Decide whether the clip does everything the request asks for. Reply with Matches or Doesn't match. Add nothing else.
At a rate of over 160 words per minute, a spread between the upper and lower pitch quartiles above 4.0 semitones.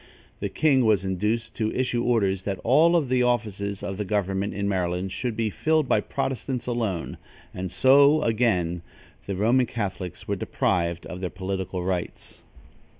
Doesn't match